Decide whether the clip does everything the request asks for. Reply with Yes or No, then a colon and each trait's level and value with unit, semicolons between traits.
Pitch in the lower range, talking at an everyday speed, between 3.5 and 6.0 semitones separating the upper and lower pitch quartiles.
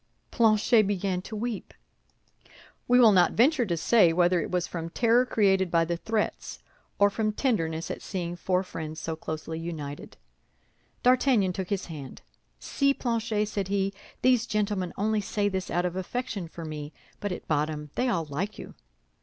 No: high, 190 Hz; average, 170 wpm; average, 4.6 semitones